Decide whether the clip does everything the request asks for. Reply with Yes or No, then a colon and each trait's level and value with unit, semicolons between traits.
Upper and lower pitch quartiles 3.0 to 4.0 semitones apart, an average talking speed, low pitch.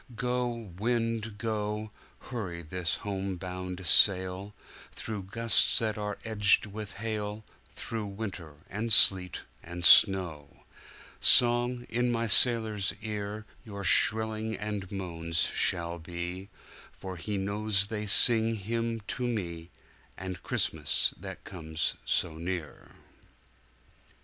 No: average, 3.3 semitones; slow, 100 wpm; low, 105 Hz